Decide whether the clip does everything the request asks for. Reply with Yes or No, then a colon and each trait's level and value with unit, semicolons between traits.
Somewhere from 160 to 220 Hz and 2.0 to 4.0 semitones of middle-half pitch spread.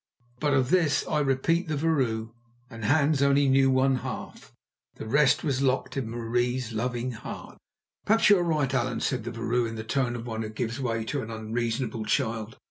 No: low, 125 Hz; average, 3.6 semitones